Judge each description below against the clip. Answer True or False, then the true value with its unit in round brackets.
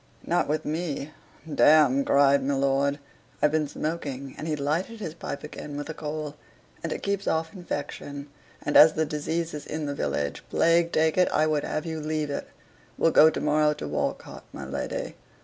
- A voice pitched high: False (150 Hz)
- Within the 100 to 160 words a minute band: False (190 wpm)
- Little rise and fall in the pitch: True (2.0 semitones)